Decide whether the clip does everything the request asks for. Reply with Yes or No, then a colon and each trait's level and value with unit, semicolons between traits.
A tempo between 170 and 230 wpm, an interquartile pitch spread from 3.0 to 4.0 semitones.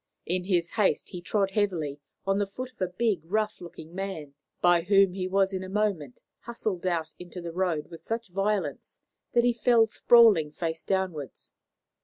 Yes: average, 180 wpm; average, 3.5 semitones